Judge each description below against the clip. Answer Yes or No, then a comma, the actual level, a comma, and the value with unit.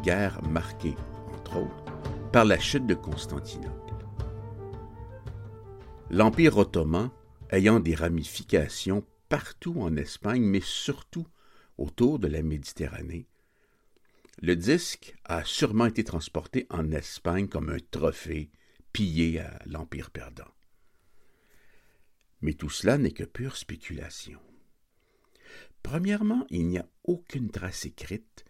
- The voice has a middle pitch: No, low, 100 Hz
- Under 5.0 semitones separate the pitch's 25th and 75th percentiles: No, wide, 5.4 semitones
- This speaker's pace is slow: Yes, slow, 110 wpm